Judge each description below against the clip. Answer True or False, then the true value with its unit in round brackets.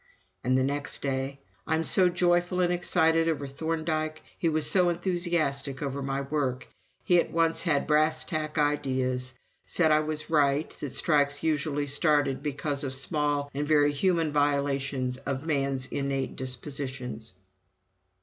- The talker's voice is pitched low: False (145 Hz)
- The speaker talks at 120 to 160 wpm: True (145 wpm)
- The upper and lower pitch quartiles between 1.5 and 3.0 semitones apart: True (2.7 semitones)